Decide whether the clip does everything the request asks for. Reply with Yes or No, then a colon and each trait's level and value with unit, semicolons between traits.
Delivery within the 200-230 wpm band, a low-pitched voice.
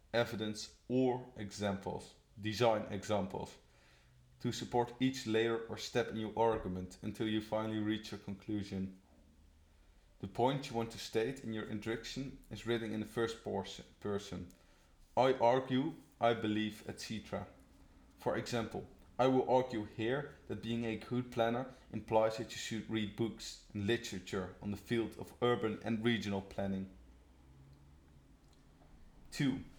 No: slow, 135 wpm; low, 110 Hz